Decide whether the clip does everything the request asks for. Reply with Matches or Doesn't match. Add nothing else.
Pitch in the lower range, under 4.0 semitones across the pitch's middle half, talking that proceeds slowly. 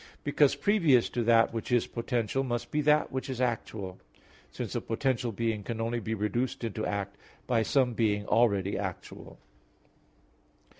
Doesn't match